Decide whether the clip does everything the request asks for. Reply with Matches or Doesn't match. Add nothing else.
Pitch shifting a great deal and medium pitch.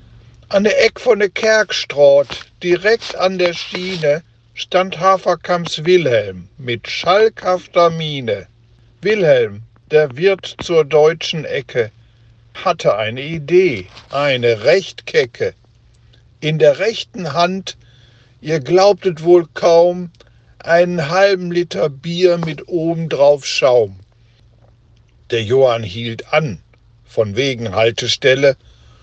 Matches